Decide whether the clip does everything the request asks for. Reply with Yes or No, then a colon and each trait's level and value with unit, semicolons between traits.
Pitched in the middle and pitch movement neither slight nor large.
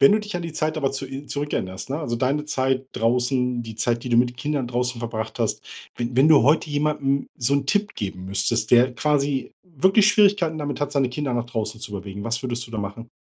No: low, 130 Hz; average, 3.9 semitones